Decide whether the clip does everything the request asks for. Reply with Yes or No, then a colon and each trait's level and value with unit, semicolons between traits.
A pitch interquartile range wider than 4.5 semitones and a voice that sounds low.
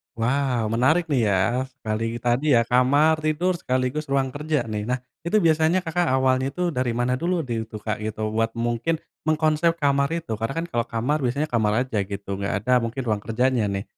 Yes: average, 5.0 semitones; low, 125 Hz